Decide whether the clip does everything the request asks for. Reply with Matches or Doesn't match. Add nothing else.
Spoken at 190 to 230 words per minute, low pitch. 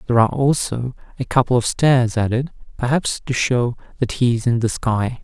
Matches